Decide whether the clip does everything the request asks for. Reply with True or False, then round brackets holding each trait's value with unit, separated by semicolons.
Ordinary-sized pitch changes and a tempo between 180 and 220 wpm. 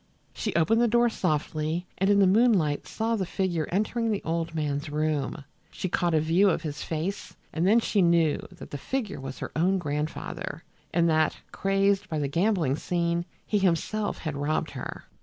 True (4.4 semitones; 185 wpm)